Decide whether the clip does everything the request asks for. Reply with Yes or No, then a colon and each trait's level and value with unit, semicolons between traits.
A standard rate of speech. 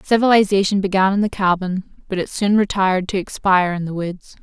Yes: average, 190 wpm